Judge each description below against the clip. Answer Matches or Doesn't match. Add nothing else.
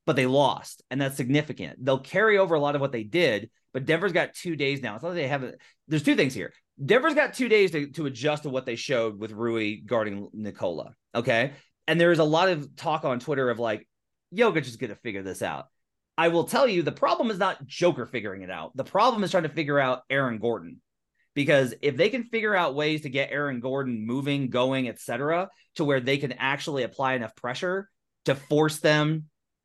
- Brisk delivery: Matches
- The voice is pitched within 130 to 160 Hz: Matches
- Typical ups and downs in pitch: Matches